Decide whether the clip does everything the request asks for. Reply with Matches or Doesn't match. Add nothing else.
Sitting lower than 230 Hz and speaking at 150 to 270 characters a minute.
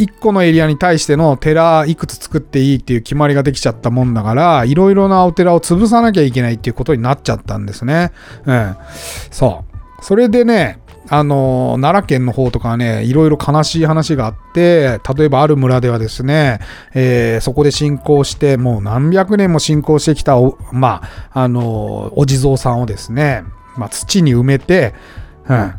Doesn't match